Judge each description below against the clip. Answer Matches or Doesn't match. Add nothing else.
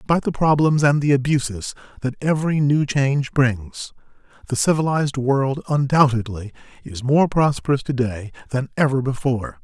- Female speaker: Doesn't match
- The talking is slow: Doesn't match